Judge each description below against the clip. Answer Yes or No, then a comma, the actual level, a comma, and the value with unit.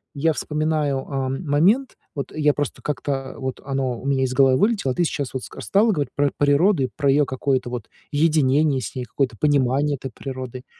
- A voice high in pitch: No, medium, 140 Hz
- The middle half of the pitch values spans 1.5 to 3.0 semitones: Yes, narrow, 2.4 semitones